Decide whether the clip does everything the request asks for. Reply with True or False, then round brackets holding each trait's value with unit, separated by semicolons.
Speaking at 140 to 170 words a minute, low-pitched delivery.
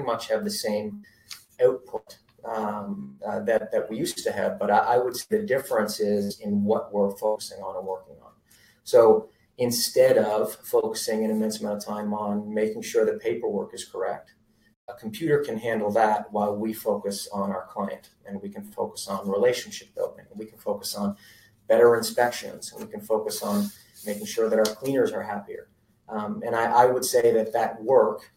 False (190 wpm; 115 Hz)